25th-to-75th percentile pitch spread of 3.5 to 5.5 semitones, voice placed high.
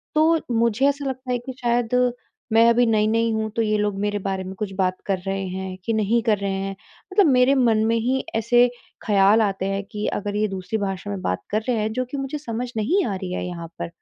Yes: average, 3.8 semitones; high, 220 Hz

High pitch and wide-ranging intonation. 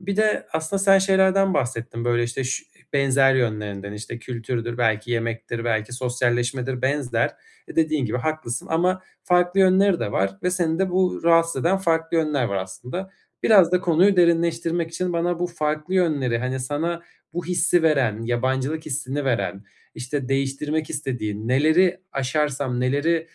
No: medium, 145 Hz; wide, 5.9 semitones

